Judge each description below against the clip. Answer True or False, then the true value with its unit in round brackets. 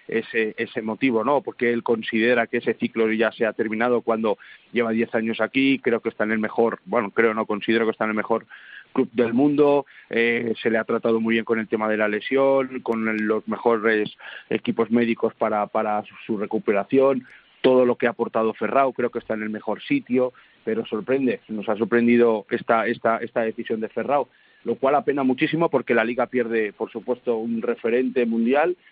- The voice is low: True (115 Hz)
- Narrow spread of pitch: True (1.7 semitones)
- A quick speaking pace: True (200 wpm)